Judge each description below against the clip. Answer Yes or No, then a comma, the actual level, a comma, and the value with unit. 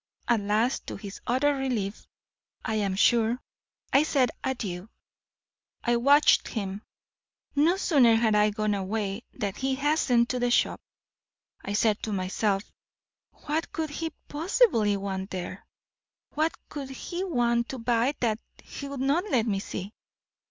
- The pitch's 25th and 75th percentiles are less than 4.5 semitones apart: No, average, 5.2 semitones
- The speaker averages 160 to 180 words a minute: No, average, 145 wpm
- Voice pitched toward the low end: No, high, 235 Hz